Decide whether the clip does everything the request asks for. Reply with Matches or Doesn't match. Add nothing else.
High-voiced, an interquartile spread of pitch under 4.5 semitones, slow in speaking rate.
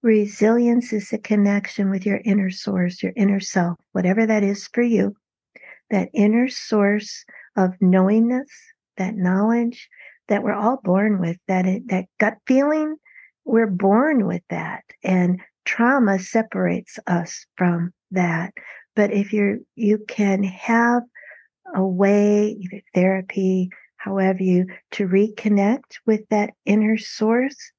Matches